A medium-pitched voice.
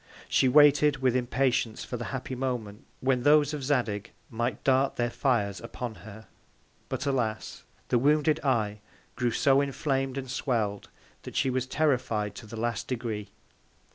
No: low, 125 Hz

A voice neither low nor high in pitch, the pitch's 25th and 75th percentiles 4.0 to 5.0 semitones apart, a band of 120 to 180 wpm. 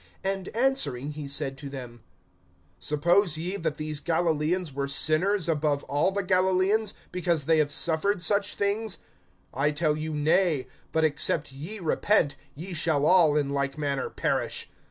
Yes: medium, 160 Hz; average, 4.3 semitones; average, 155 wpm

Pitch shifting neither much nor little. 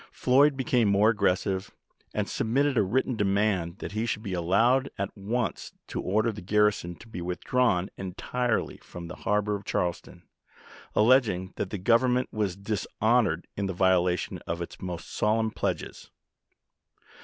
Yes: average, 3.9 semitones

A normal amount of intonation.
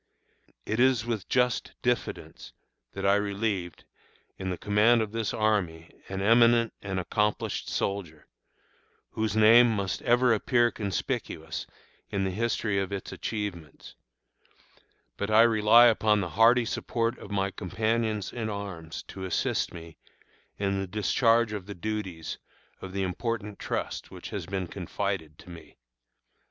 Yes: average, 3.2 semitones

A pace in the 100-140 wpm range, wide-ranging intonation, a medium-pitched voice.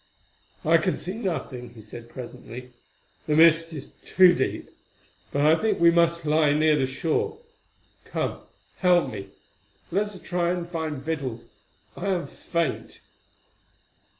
No: slow, 135 wpm; average, 4.6 semitones; medium, 160 Hz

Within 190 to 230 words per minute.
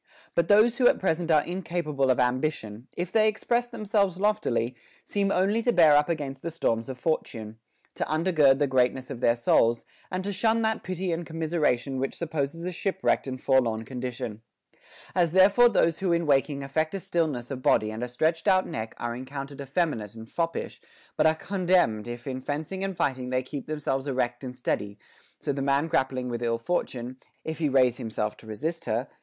Yes: average, 200 wpm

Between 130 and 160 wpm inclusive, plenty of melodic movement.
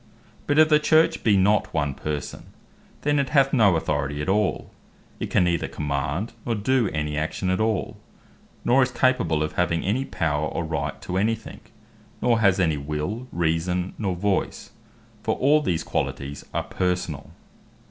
No: average, 170 wpm; wide, 6.7 semitones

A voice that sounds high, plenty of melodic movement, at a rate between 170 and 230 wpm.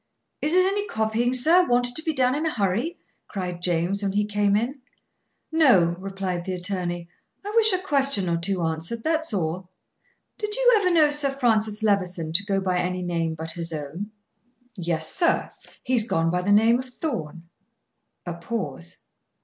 Yes: high, 205 Hz; wide, 7.4 semitones; average, 180 wpm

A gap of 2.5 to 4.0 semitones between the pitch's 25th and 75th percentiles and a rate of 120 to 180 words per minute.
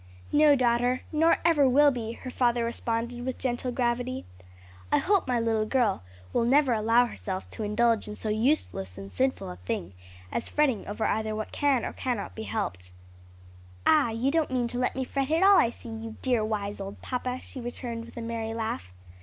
No: average, 2.8 semitones; average, 200 wpm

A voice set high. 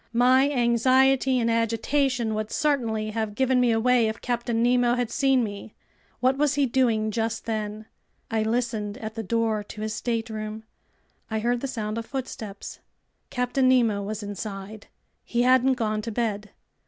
Yes: high, 230 Hz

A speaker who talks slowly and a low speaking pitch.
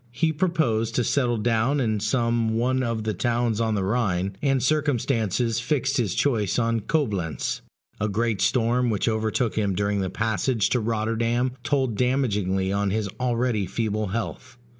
No: average, 160 wpm; low, 115 Hz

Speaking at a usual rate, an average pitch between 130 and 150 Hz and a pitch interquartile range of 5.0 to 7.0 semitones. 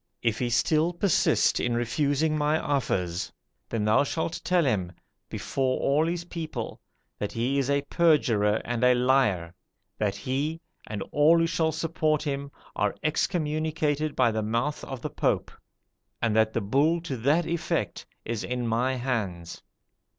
Yes: average, 155 wpm; low, 135 Hz; average, 5.3 semitones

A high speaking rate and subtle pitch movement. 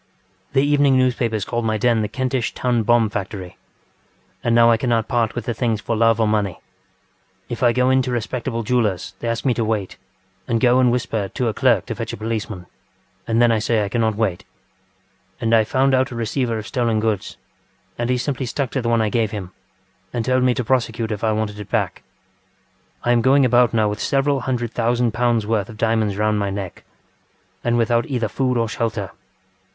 Yes: fast, 210 wpm; narrow, 2.2 semitones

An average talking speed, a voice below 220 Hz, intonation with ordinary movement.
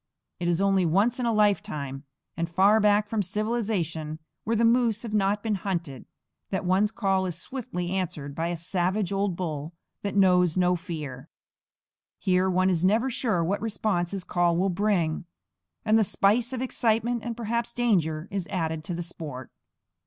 Yes: average, 175 wpm; high, 190 Hz; average, 3.9 semitones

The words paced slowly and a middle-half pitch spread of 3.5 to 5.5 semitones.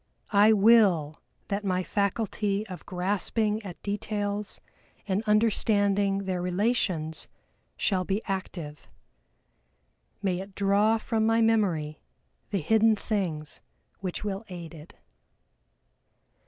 No: slow, 105 wpm; average, 2.7 semitones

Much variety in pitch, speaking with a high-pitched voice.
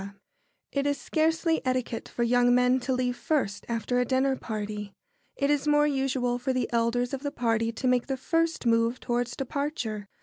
No: average, 2.8 semitones; very high, 250 Hz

